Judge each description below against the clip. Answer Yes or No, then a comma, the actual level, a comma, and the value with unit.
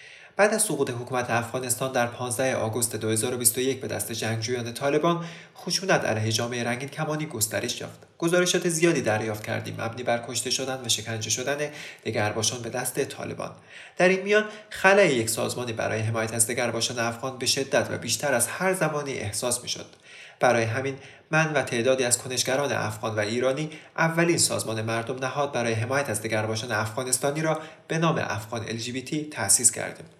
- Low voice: Yes, low, 125 Hz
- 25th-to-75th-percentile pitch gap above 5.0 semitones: No, average, 4.6 semitones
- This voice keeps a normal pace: Yes, average, 165 wpm